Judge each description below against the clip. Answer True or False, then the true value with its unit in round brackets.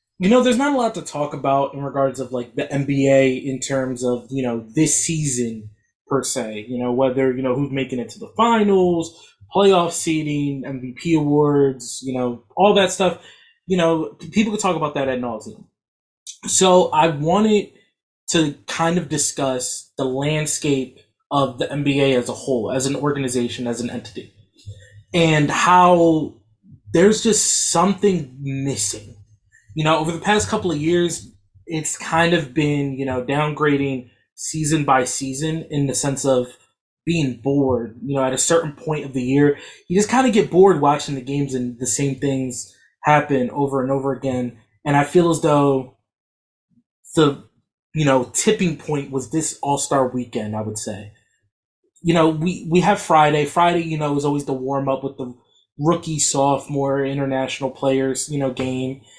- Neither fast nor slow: True (170 wpm)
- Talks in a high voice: False (140 Hz)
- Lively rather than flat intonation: False (3.8 semitones)